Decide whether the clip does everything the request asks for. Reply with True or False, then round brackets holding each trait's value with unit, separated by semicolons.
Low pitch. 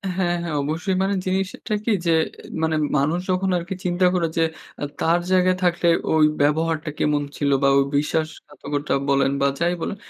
False (165 Hz)